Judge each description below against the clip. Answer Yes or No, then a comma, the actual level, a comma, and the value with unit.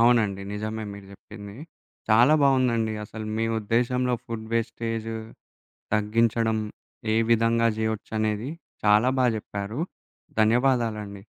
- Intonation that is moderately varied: No, narrow, 1.5 semitones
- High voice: No, low, 110 Hz